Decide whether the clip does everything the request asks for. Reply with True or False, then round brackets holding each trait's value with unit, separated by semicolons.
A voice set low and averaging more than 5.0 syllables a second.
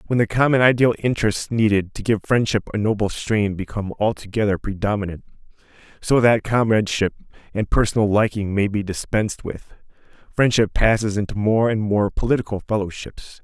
True (105 Hz; 5.6 syllables/s)